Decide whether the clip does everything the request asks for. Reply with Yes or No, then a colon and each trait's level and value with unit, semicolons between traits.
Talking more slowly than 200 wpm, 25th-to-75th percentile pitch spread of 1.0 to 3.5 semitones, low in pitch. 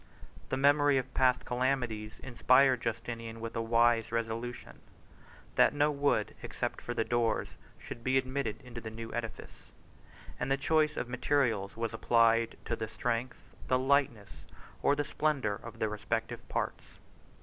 Yes: average, 155 wpm; average, 2.7 semitones; low, 120 Hz